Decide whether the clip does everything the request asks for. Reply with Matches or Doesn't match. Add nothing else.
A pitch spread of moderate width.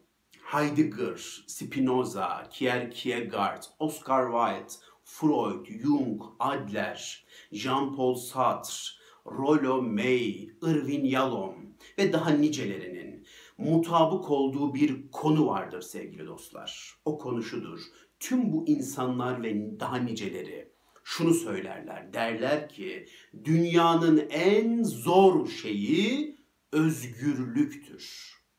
Doesn't match